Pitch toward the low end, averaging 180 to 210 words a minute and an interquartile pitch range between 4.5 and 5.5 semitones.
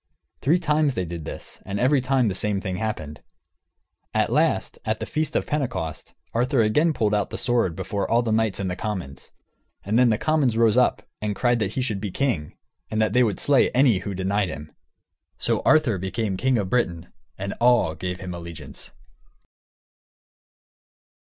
Yes: low, 110 Hz; average, 185 wpm; average, 5.1 semitones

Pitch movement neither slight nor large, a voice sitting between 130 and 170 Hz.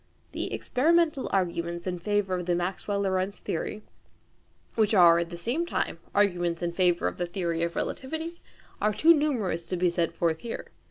No: average, 4.0 semitones; medium, 185 Hz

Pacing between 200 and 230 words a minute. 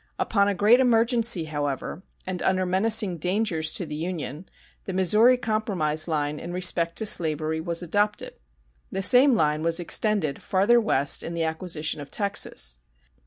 No: average, 155 wpm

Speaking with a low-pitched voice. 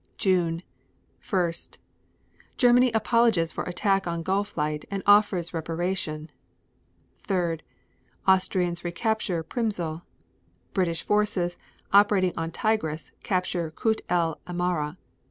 No: medium, 180 Hz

